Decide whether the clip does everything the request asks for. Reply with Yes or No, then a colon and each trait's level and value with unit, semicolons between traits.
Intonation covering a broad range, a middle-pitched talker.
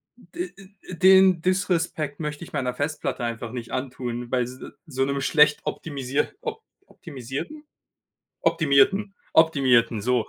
Yes: wide, 5.9 semitones; medium, 145 Hz